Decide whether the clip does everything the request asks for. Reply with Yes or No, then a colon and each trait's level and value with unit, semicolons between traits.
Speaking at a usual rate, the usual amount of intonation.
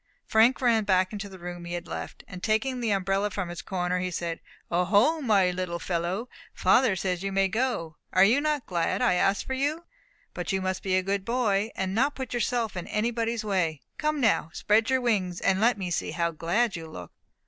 No: fast, 215 wpm; average, 4.5 semitones